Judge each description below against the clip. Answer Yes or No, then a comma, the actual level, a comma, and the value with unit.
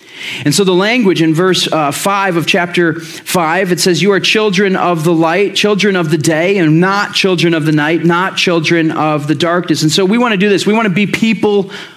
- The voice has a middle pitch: Yes, medium, 180 Hz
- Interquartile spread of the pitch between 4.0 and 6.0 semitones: No, average, 3.2 semitones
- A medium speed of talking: No, fast, 230 wpm